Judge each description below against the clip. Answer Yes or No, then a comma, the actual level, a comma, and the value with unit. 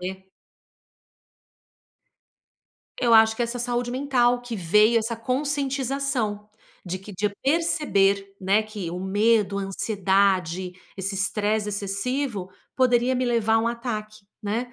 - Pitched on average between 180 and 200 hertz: No, high, 220 Hz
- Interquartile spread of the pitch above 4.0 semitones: No, average, 3.7 semitones